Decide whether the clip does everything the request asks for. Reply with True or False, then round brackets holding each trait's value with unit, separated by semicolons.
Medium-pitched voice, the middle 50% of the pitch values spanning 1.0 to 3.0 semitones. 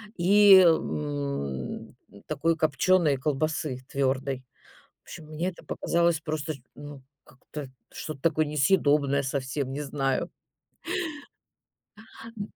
True (145 Hz; 2.7 semitones)